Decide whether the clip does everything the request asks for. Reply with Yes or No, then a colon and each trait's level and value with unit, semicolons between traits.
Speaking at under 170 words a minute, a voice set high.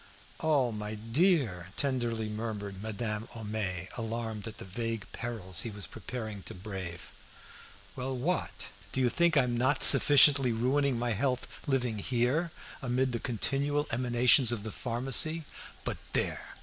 No: average, 140 wpm; low, 120 Hz